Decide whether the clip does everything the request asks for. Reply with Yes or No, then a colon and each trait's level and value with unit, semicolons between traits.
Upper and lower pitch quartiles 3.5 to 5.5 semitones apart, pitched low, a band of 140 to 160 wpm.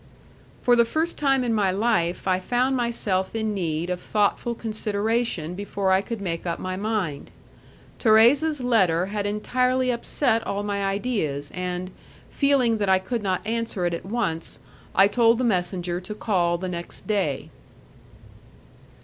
No: average, 4.3 semitones; high, 205 Hz; average, 155 wpm